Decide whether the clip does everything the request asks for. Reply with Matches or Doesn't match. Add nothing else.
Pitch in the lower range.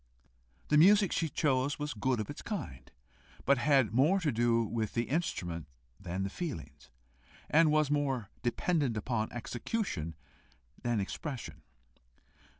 Matches